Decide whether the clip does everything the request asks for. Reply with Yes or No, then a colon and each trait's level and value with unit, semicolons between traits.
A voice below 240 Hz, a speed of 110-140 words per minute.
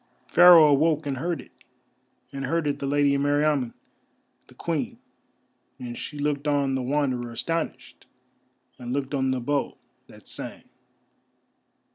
Yes: medium, 140 Hz; slow, 135 wpm